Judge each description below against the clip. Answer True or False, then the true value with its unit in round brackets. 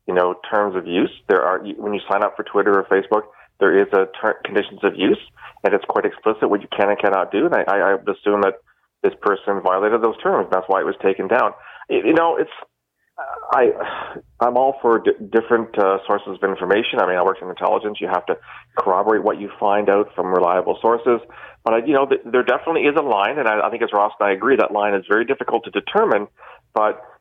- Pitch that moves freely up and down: True (7.3 semitones)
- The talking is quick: True (225 wpm)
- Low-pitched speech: True (115 Hz)